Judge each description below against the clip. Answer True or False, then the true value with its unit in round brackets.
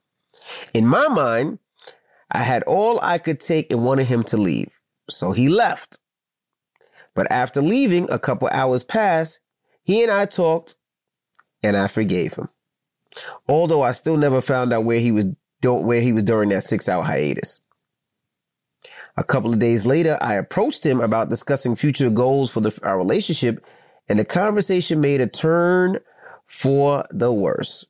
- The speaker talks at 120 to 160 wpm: True (155 wpm)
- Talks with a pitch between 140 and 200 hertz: False (130 Hz)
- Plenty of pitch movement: True (5.7 semitones)